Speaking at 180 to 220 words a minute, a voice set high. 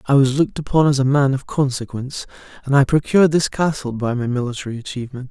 No: fast, 205 wpm; low, 135 Hz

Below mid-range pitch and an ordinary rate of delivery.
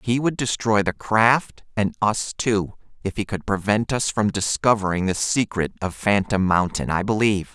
Yes: low, 105 Hz; average, 175 wpm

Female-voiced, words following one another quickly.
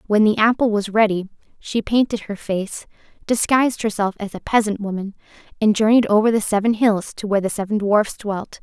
No: female; average, 190 wpm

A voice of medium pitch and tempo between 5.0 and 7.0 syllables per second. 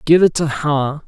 No: medium, 150 Hz; 4.2 syllables/s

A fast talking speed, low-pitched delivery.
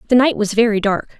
No: fast, 250 wpm; high, 220 Hz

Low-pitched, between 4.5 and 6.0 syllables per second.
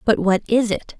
No: high, 215 Hz; 4.8 syllables/s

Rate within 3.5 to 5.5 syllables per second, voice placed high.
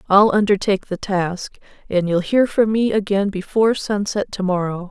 Yes: 5.0 syllables/s; high, 200 Hz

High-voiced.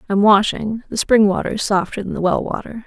Yes: high, 210 Hz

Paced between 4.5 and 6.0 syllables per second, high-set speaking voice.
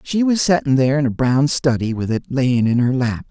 No: 5.4 syllables/s; low, 135 Hz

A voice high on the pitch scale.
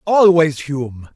No: medium, 155 Hz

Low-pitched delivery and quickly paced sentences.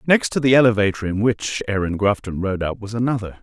Yes: low, 110 Hz; fast, 210 wpm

